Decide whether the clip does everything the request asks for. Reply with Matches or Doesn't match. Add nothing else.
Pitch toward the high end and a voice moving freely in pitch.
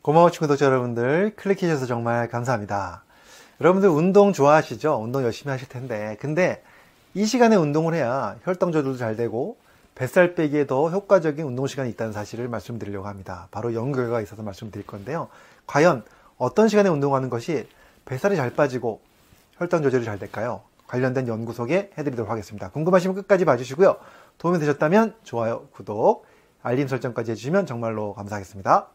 Doesn't match